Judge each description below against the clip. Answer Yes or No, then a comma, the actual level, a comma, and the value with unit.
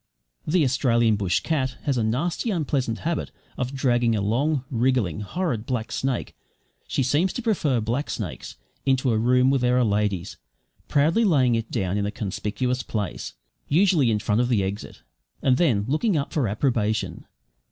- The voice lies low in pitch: Yes, low, 125 Hz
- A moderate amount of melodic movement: Yes, average, 4.5 semitones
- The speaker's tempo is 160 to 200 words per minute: Yes, average, 170 wpm